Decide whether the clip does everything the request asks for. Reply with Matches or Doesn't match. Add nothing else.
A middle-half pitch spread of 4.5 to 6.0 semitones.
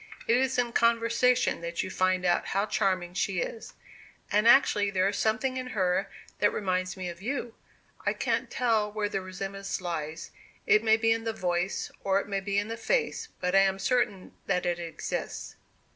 Doesn't match